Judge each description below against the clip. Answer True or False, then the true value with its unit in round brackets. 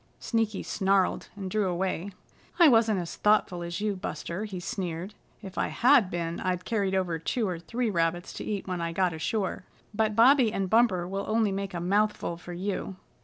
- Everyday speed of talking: True (190 wpm)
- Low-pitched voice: False (195 Hz)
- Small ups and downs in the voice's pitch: False (3.3 semitones)